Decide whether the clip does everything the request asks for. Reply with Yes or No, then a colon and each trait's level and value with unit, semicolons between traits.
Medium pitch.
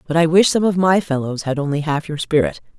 Yes: medium, 160 Hz